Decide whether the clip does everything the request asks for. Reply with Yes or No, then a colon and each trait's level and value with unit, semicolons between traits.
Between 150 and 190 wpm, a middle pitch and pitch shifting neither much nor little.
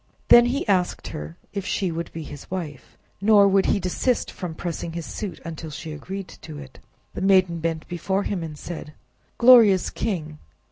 Yes: average, 180 wpm; medium, 175 Hz; average, 3.7 semitones